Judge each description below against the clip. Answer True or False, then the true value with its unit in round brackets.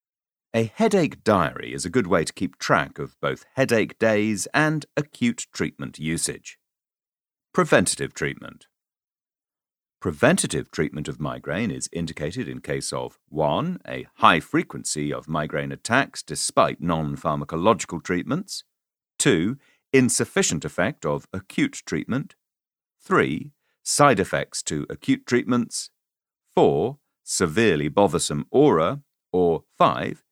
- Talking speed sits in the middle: False (115 wpm)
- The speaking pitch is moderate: False (110 Hz)